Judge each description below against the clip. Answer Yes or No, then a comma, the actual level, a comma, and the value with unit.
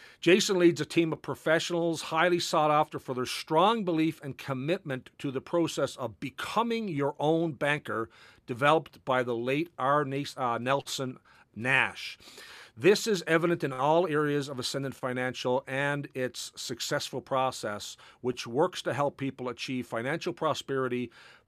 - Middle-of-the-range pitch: Yes, medium, 145 Hz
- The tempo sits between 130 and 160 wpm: Yes, average, 145 wpm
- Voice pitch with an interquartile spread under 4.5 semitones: Yes, average, 3.9 semitones